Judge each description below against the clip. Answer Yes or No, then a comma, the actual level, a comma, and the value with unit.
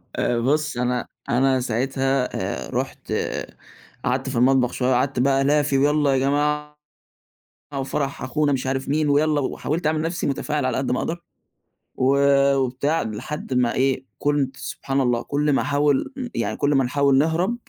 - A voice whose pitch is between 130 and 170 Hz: Yes, low, 135 Hz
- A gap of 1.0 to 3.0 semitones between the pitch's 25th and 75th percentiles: Yes, narrow, 2.4 semitones